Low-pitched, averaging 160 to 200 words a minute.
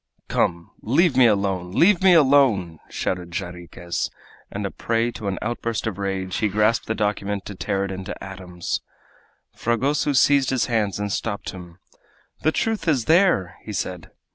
Yes: low, 105 Hz; average, 165 wpm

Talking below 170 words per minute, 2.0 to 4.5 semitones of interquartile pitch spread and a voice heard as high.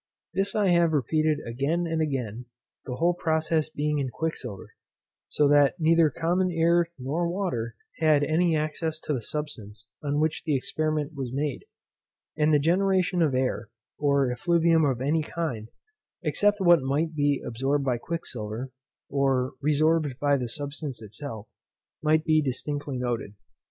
No: average, 150 wpm; average, 3.6 semitones; medium, 150 Hz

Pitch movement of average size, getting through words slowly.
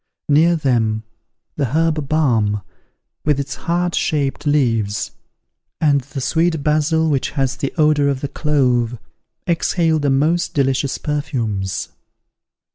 Yes: average, 3.4 semitones; slow, 120 wpm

